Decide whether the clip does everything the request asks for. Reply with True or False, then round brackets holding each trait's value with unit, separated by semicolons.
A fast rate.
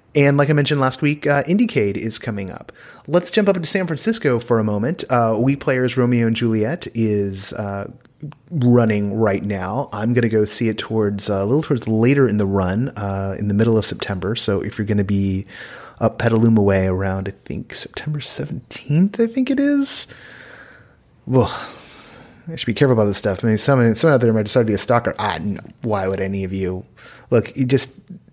True (210 wpm)